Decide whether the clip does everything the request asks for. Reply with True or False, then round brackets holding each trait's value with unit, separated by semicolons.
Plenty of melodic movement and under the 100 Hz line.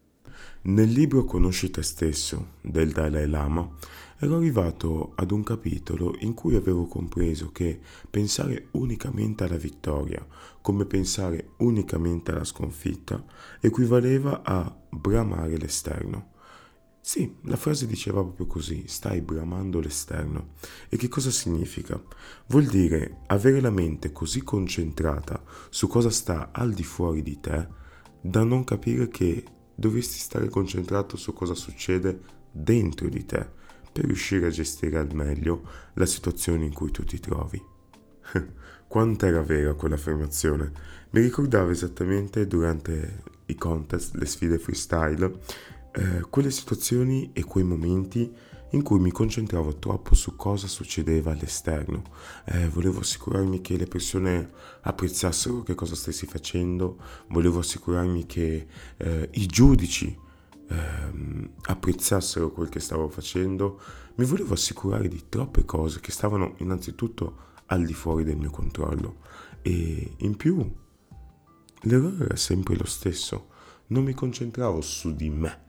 False (4.2 semitones; 90 Hz)